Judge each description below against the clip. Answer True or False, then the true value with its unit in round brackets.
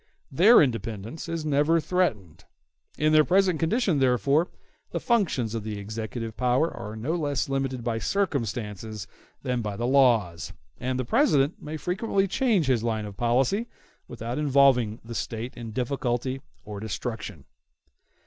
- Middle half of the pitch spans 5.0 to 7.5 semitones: True (5.5 semitones)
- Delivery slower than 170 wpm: True (145 wpm)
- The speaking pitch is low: True (130 Hz)